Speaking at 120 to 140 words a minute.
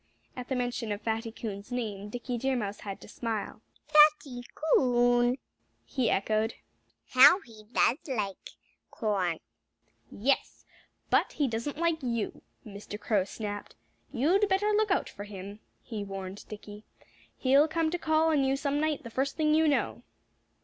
No: average, 155 wpm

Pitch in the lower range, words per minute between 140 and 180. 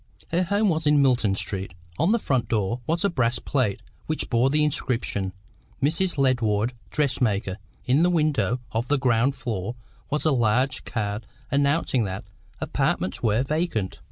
Yes: low, 130 Hz; average, 155 wpm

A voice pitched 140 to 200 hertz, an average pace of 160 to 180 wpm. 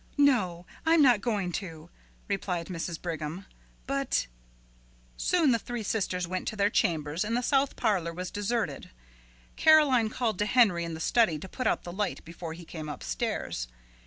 Yes: high, 190 Hz; average, 170 wpm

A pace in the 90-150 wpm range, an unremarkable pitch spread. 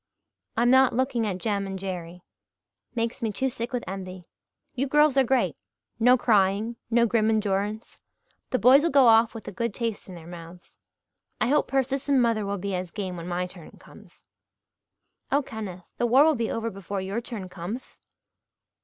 No: average, 180 wpm; average, 4.6 semitones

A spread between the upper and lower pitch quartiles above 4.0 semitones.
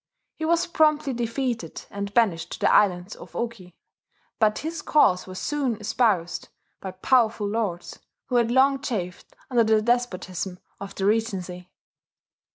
Yes: average, 4.9 semitones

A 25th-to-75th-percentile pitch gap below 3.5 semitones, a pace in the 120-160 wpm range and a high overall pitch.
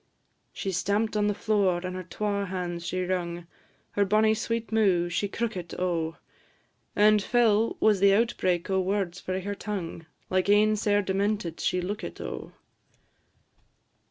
Yes: narrow, 2.6 semitones; average, 150 wpm; high, 195 Hz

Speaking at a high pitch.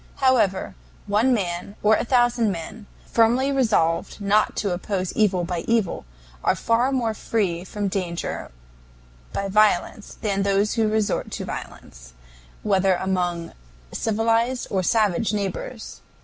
Yes: high, 205 Hz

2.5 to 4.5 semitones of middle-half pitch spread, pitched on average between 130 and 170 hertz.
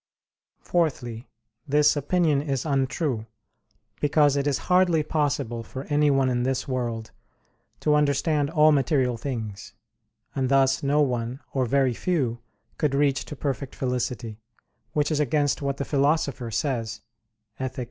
Yes: average, 2.9 semitones; medium, 140 Hz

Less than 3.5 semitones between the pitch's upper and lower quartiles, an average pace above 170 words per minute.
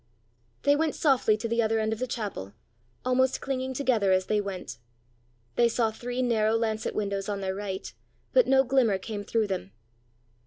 No: average, 3.9 semitones; average, 180 wpm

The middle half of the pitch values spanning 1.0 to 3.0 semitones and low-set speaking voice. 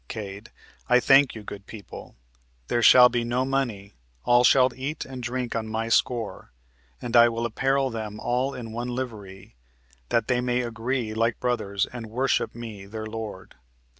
Yes: narrow, 2.4 semitones; low, 120 Hz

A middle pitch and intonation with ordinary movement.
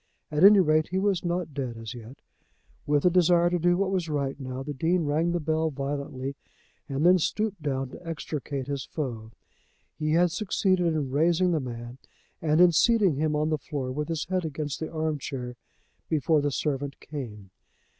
Yes: medium, 155 Hz; average, 4.0 semitones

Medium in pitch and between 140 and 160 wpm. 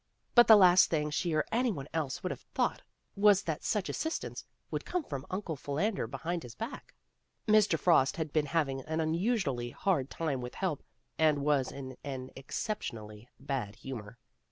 No: medium, 155 Hz; average, 180 wpm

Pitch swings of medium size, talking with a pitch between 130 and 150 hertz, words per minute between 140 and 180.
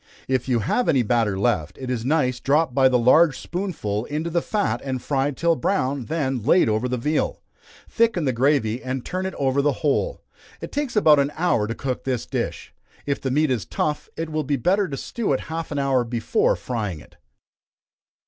No: average, 4.4 semitones; low, 135 Hz; fast, 205 wpm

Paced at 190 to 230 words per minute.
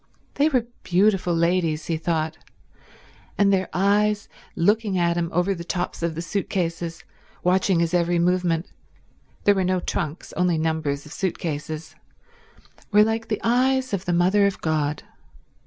No: average, 150 wpm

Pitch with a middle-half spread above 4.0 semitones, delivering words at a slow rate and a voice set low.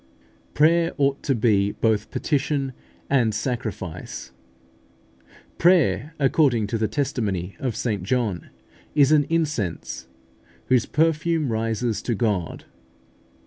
Yes: wide, 5.6 semitones; slow, 105 wpm; low, 125 Hz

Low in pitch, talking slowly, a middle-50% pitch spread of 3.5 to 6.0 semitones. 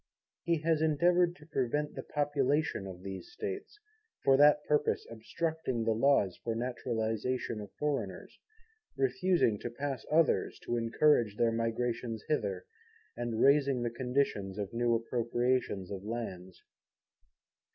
Yes: low, 125 Hz; slow, 130 wpm; average, 4.7 semitones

